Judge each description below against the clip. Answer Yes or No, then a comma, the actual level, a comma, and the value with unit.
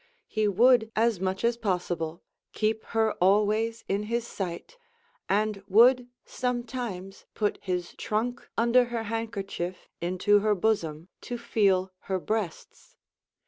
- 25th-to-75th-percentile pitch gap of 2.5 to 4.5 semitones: Yes, average, 3.5 semitones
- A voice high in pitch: Yes, high, 215 Hz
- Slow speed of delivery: Yes, slow, 125 wpm